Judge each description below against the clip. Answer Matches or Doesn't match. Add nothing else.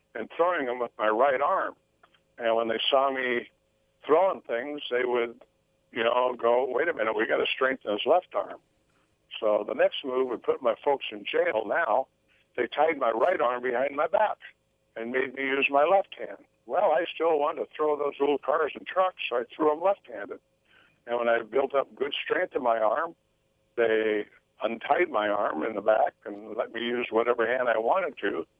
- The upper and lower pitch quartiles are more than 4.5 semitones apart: Doesn't match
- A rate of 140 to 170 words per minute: Doesn't match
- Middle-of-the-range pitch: Doesn't match